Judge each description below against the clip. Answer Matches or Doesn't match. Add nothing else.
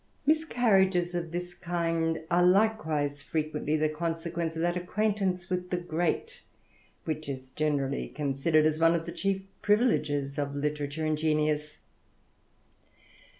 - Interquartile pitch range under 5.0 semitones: Matches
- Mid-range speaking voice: Matches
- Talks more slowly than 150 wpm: Matches